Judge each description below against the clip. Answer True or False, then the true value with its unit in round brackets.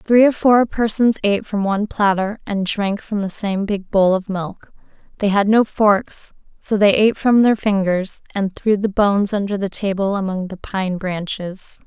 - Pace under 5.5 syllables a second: True (4.6 syllables/s)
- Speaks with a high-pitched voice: True (200 Hz)